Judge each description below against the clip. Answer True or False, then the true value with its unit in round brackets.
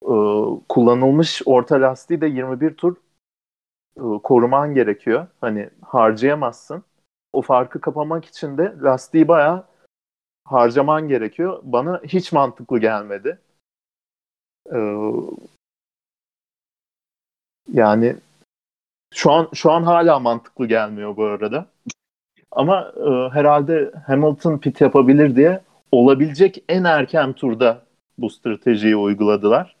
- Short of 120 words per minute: True (95 wpm)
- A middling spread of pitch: False (5.9 semitones)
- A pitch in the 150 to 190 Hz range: False (135 Hz)